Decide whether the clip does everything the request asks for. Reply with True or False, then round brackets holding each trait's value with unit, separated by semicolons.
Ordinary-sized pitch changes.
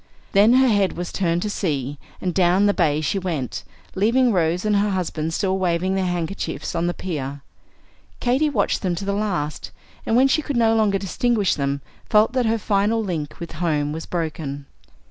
True (4.6 semitones)